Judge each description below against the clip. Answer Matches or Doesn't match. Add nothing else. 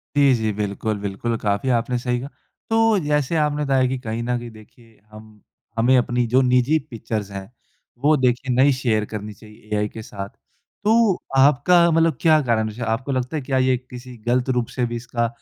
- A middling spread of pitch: Matches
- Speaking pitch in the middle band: Doesn't match